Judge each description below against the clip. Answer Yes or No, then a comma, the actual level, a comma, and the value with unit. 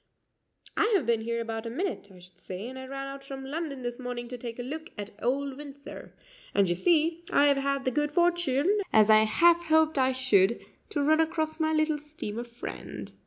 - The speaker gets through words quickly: Yes, fast, 215 wpm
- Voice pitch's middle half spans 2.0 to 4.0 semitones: No, average, 5.0 semitones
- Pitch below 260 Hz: No, very high, 275 Hz